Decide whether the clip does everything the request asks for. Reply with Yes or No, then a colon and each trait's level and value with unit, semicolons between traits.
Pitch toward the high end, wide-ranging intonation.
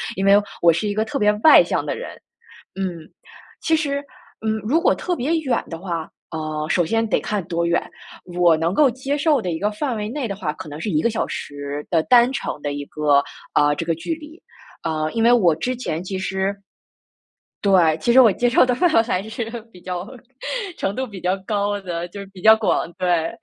Yes: high, 195 Hz; wide, 5.9 semitones